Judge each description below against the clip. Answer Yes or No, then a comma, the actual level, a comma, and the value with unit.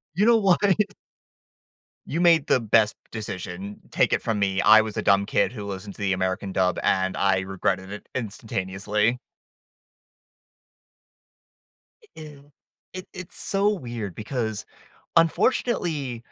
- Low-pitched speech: Yes, low, 110 Hz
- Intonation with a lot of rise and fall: Yes, wide, 7.0 semitones